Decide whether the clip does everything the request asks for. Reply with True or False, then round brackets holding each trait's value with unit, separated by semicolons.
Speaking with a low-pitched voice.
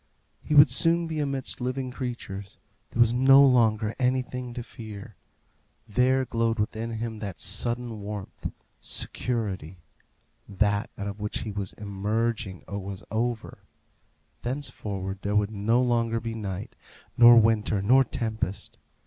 True (115 Hz)